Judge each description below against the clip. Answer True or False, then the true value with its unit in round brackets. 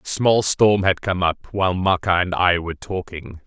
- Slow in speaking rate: False (210 wpm)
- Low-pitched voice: True (90 Hz)